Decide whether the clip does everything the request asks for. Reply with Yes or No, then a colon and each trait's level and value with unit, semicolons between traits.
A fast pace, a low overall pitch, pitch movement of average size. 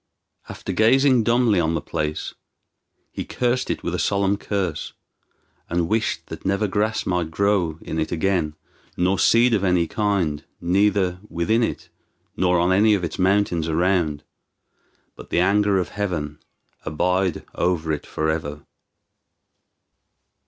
No: average, 140 wpm; very low, 90 Hz; average, 3.8 semitones